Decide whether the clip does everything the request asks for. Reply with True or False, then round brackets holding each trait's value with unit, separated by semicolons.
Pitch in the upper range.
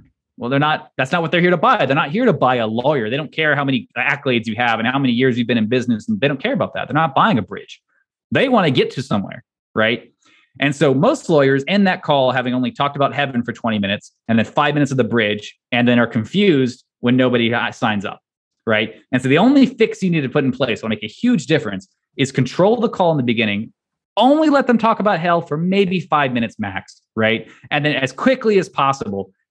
False (135 Hz)